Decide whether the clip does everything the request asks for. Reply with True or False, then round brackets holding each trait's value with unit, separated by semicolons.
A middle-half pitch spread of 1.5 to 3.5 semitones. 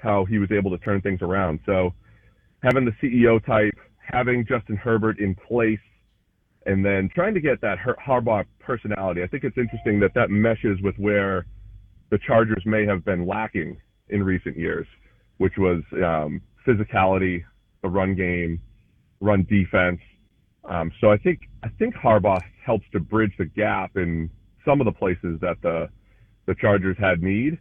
True (2.8 semitones)